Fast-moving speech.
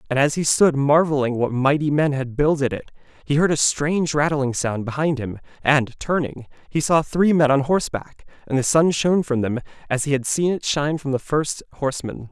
Yes: fast, 210 wpm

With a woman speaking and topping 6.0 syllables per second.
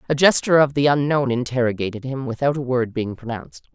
Yes: female; 6.3 syllables/s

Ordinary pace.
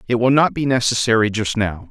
No: fast, 220 wpm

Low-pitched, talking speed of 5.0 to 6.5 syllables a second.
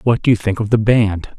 Yes: low, 110 Hz; 5.4 syllables/s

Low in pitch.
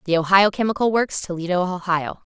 No: high, 190 Hz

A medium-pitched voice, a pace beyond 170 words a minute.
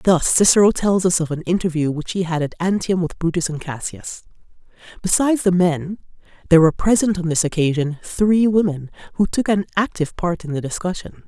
Yes: medium, 175 Hz; average, 185 wpm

